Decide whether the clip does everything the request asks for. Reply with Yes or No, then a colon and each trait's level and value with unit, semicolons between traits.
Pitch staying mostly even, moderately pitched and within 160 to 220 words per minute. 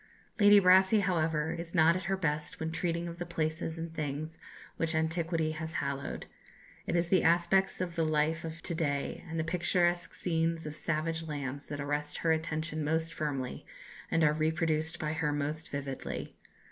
Yes: narrow, 1.7 semitones; medium, 160 Hz; average, 175 wpm